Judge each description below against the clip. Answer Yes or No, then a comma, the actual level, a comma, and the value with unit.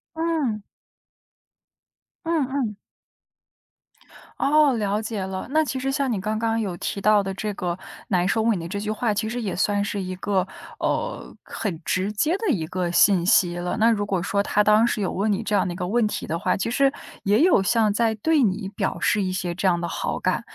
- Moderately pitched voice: No, high, 210 Hz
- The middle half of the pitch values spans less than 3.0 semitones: No, average, 3.4 semitones